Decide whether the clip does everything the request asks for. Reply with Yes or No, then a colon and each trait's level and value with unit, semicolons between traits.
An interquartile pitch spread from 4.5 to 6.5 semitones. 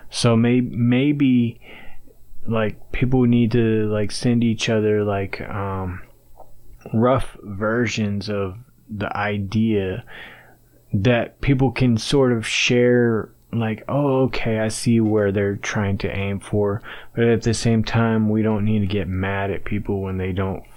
No: average, 2.9 semitones